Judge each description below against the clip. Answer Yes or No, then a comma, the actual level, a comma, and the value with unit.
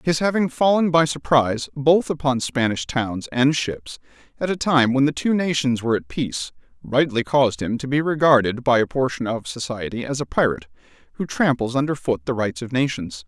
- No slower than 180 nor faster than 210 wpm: Yes, average, 195 wpm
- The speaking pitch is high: No, low, 130 Hz